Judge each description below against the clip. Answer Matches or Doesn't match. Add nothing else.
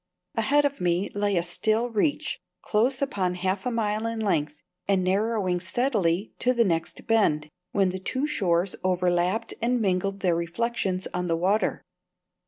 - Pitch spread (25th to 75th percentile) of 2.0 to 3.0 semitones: Doesn't match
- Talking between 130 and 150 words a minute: Doesn't match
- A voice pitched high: Matches